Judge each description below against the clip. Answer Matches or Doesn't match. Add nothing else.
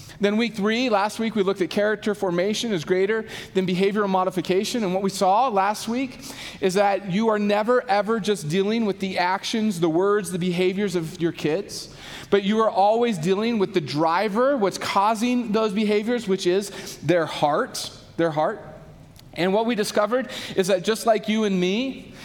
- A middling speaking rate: Matches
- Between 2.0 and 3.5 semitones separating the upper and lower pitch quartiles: Matches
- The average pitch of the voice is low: Doesn't match